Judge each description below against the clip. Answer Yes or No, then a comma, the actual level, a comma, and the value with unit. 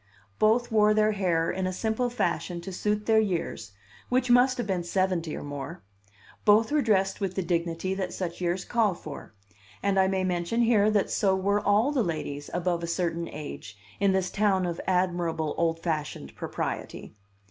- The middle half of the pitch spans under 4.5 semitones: Yes, average, 3.8 semitones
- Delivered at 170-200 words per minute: Yes, average, 180 wpm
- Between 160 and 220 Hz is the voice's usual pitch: Yes, high, 190 Hz